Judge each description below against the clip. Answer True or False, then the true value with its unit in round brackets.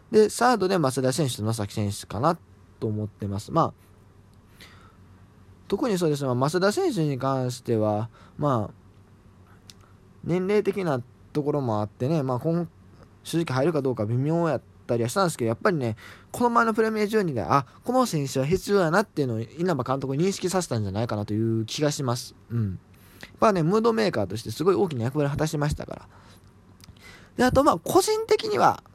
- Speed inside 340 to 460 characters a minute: True (370 characters per minute)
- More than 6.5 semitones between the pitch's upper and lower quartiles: True (8.5 semitones)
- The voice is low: True (125 Hz)